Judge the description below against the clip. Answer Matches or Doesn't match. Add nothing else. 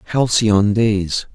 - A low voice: Matches